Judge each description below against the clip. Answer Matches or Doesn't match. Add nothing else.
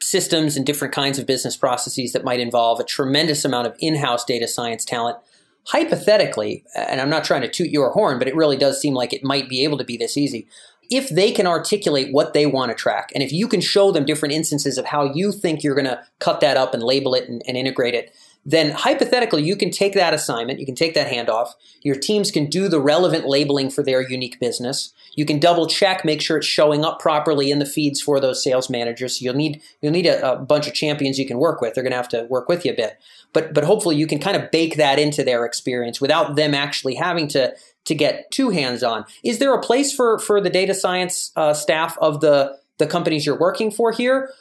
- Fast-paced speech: Matches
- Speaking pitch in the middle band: Matches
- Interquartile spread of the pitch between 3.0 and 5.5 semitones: Matches